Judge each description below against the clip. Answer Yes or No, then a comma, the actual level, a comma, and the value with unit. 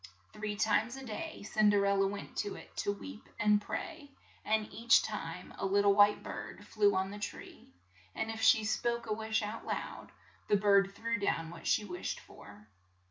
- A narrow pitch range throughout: Yes, narrow, 1.8 semitones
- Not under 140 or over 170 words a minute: No, average, 200 wpm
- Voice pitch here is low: No, high, 205 Hz